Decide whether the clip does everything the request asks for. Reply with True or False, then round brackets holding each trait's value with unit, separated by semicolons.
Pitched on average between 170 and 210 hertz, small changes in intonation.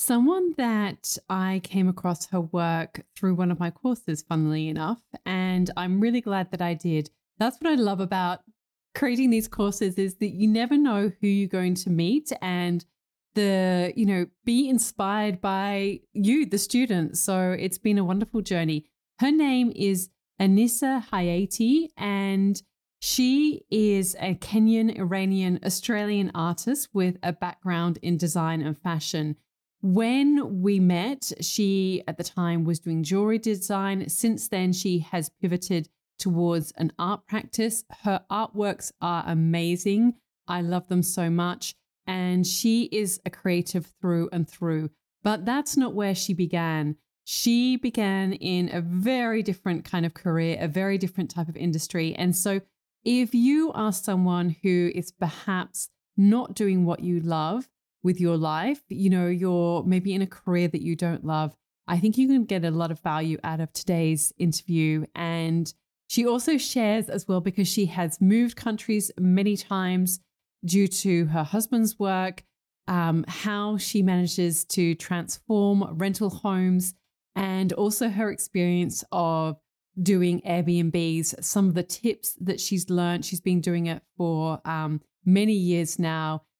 False (185 Hz; 3.3 semitones)